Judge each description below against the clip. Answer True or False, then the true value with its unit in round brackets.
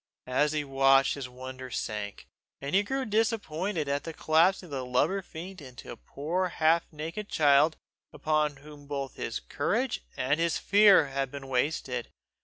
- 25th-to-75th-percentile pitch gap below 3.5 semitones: False (3.8 semitones)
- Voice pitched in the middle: True (150 Hz)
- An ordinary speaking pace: True (165 wpm)